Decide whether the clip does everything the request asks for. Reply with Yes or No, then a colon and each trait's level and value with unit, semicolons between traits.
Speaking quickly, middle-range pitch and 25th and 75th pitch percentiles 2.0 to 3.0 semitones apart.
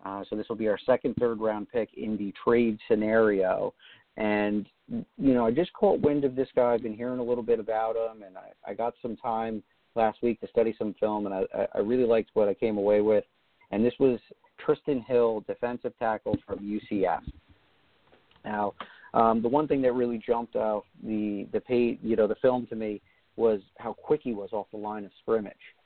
No: fast, 210 wpm; low, 115 Hz; narrow, 2.4 semitones